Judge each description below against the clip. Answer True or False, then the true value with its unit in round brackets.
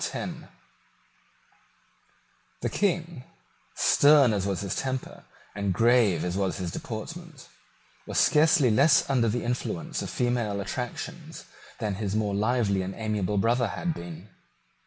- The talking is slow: True (125 wpm)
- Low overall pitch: True (110 Hz)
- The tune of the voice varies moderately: True (4.4 semitones)